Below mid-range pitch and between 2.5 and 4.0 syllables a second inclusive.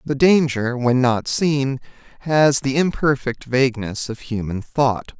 Yes: low, 130 Hz; 3.9 syllables/s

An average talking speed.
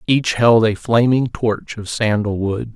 Yes: average, 175 wpm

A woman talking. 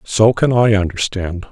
No: male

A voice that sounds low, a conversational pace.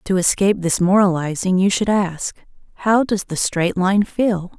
No: high, 190 Hz; average, 170 wpm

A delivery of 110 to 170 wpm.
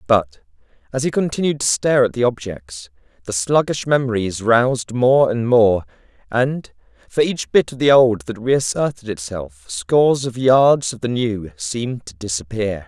Yes: average, 165 wpm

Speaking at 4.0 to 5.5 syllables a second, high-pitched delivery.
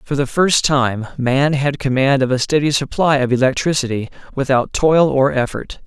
No: 4.8 syllables/s; low, 135 Hz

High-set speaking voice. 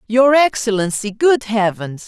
Yes: high, 225 Hz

